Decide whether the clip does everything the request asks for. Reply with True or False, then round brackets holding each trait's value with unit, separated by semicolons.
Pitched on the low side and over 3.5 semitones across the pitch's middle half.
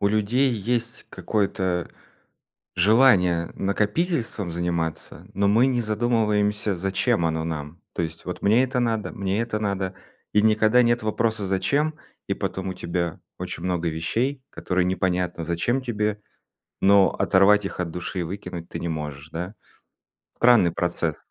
True (100 Hz; 4.4 semitones)